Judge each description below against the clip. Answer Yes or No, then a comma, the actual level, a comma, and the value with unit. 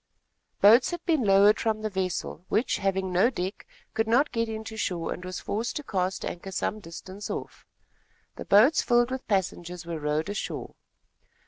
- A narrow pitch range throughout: No, average, 3.8 semitones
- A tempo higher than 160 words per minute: Yes, average, 175 wpm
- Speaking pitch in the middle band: No, high, 200 Hz